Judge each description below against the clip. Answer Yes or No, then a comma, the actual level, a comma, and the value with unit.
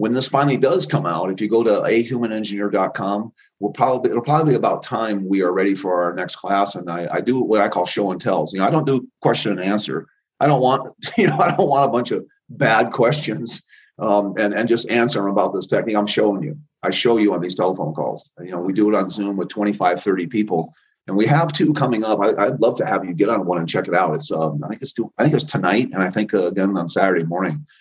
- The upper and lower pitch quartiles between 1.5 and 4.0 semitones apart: No, average, 4.4 semitones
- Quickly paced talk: Yes, fast, 265 wpm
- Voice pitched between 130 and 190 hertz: No, low, 105 Hz